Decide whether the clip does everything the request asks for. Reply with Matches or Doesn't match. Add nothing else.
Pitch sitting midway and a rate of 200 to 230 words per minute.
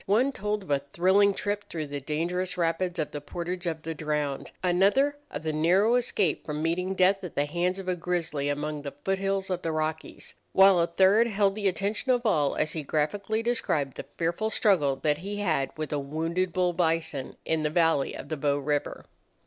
Matches